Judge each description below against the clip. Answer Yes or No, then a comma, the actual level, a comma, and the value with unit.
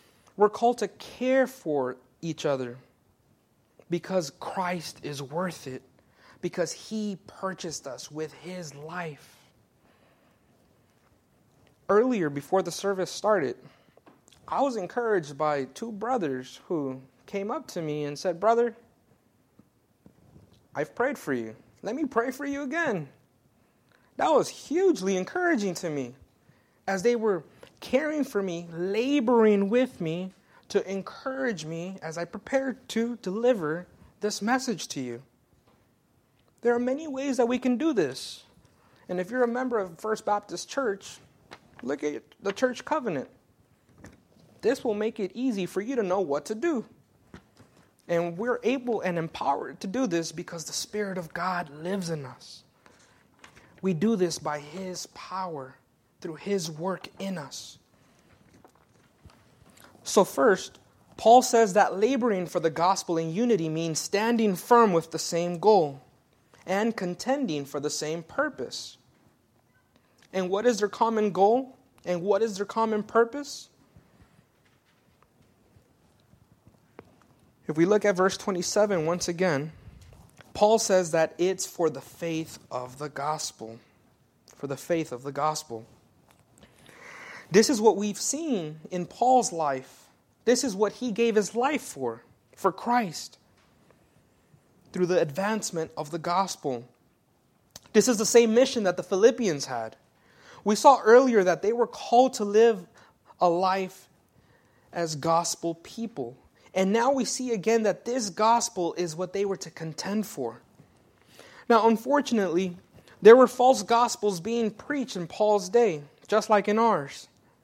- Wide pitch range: Yes, wide, 5.9 semitones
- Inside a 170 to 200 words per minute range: No, average, 140 wpm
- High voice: Yes, high, 195 Hz